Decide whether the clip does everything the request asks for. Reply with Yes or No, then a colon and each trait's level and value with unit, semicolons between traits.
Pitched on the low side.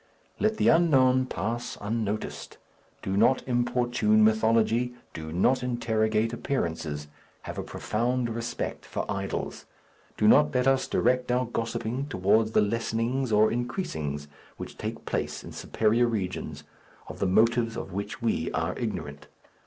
Yes: low, 115 Hz